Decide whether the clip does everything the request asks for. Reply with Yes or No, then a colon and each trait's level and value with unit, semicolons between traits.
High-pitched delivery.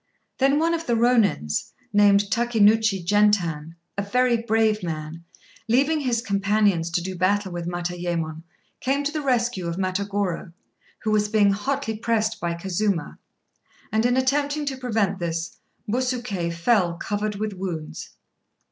Yes: high, 205 Hz